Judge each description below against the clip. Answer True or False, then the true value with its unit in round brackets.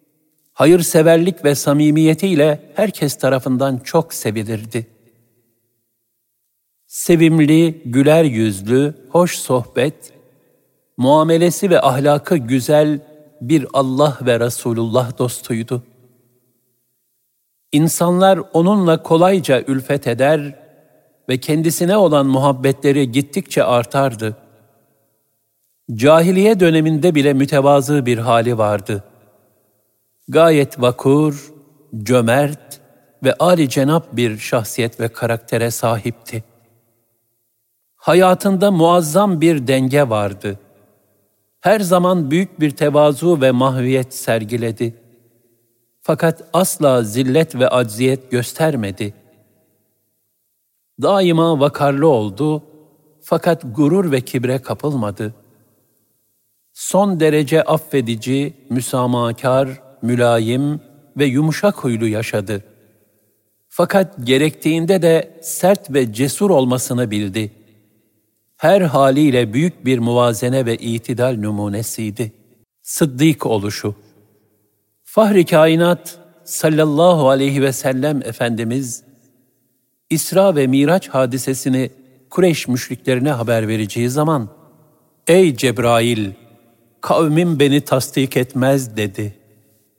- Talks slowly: True (85 wpm)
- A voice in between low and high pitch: False (130 Hz)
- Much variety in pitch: False (4.7 semitones)